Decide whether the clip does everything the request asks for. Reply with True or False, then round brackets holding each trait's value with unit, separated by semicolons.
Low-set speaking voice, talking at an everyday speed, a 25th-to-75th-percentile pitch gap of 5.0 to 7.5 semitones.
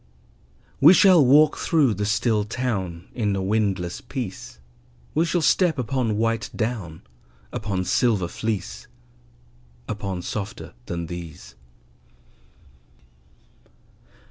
False (110 Hz; 100 wpm; 5.3 semitones)